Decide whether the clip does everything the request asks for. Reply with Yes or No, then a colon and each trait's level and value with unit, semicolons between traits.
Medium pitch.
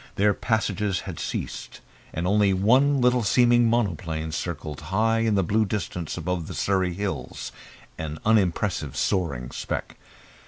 No: very low, 95 Hz